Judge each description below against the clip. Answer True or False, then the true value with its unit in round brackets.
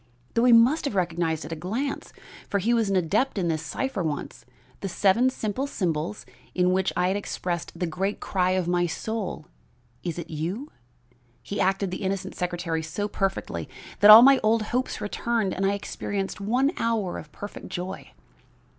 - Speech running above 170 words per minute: True (180 wpm)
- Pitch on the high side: True (195 Hz)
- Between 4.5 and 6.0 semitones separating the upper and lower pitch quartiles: False (4.0 semitones)